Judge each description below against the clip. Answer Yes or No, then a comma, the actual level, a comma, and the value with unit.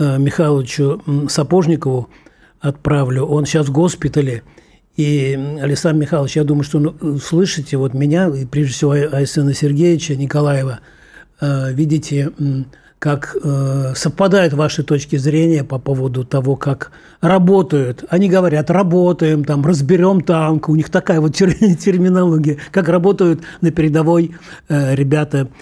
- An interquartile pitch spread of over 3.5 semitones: No, average, 3.2 semitones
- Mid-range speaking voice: Yes, medium, 150 Hz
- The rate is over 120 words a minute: No, average, 115 wpm